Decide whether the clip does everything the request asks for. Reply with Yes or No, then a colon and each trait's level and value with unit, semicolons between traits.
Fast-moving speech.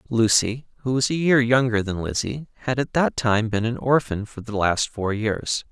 Yes: fast, 210 wpm